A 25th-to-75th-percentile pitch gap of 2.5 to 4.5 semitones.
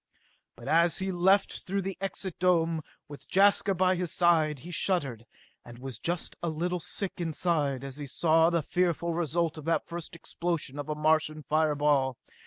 Yes: average, 2.9 semitones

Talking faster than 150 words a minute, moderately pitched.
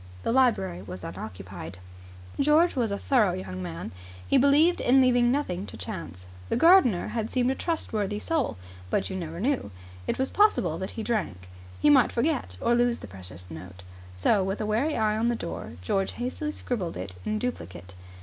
No: average, 185 wpm; high, 210 Hz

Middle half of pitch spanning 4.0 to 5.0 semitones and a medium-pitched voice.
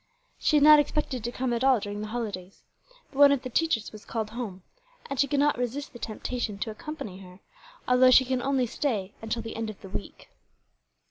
No: average, 4.3 semitones; high, 240 Hz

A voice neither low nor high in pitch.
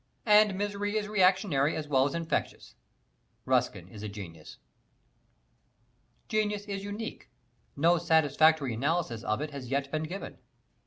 Yes: medium, 160 Hz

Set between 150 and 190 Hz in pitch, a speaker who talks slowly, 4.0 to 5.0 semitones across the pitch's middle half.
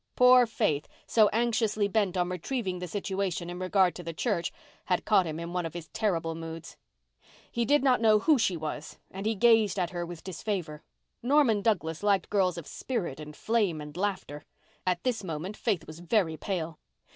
No: medium, 185 Hz; average, 190 wpm; average, 4.5 semitones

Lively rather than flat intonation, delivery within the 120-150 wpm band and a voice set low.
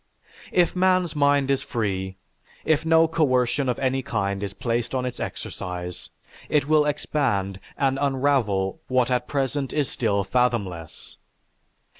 Yes: wide, 6.0 semitones; slow, 135 wpm; low, 130 Hz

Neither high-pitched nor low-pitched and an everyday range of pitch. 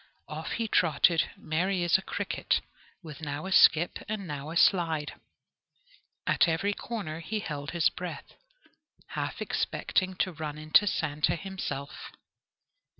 Yes: medium, 165 Hz; average, 3.7 semitones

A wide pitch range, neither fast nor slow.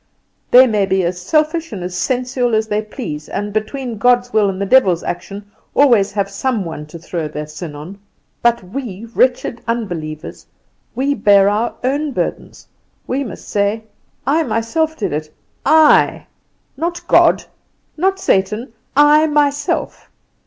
Yes: wide, 5.7 semitones; average, 150 wpm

